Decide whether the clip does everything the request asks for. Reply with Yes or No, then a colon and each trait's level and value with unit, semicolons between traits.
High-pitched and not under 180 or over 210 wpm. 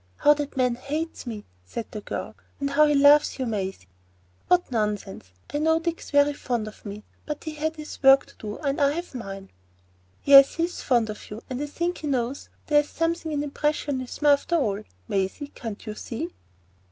Yes: very high, 280 Hz; average, 200 wpm